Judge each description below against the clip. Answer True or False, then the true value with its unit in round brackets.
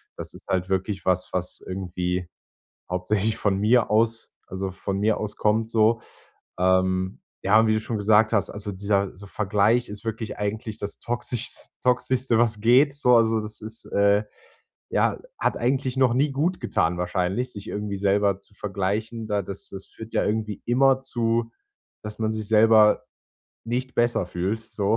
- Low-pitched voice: True (105 Hz)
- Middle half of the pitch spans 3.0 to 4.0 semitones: False (2.6 semitones)